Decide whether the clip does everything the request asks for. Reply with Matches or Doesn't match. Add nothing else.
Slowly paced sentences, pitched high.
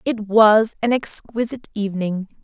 Matches